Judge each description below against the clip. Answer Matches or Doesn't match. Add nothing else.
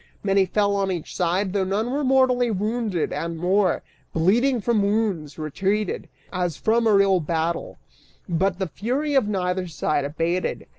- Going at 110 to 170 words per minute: Matches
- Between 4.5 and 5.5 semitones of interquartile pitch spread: Doesn't match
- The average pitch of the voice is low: Doesn't match